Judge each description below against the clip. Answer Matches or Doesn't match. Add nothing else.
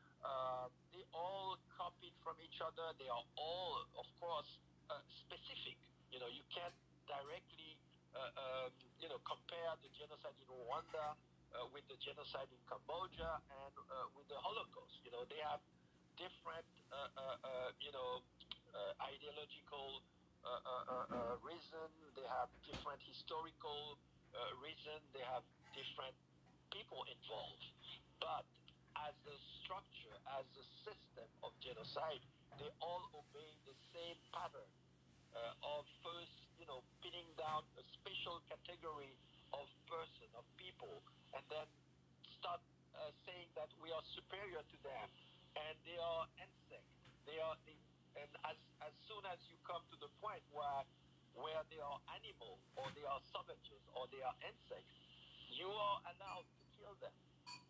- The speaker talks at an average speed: Matches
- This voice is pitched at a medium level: Matches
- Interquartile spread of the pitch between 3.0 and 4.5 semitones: Matches